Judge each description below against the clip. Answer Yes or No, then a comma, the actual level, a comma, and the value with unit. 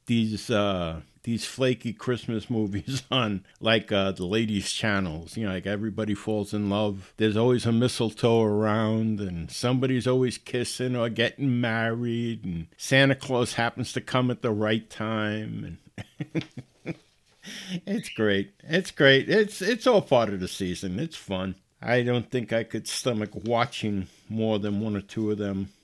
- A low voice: Yes, low, 110 Hz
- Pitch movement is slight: No, average, 3.4 semitones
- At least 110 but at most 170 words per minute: Yes, average, 160 wpm